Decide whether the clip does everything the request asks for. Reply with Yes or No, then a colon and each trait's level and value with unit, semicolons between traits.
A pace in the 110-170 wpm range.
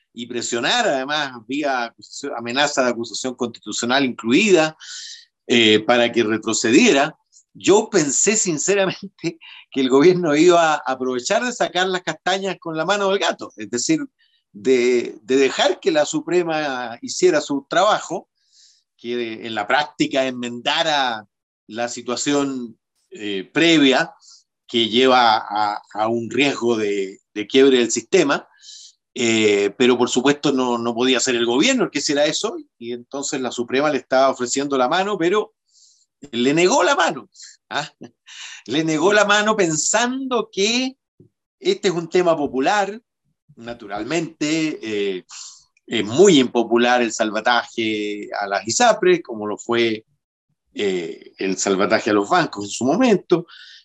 Yes: average, 140 wpm